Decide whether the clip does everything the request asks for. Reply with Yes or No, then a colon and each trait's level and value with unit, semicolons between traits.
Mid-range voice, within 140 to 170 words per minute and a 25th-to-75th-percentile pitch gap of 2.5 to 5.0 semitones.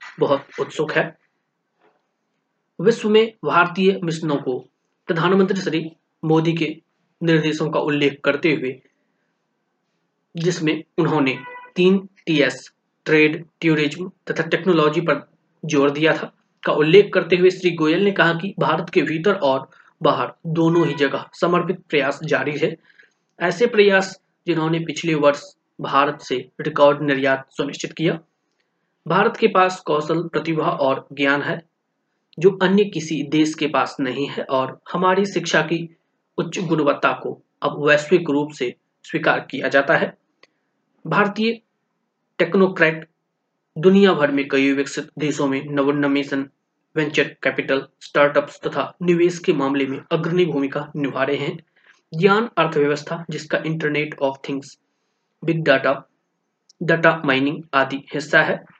No: medium, 160 Hz; average, 125 wpm; average, 4.0 semitones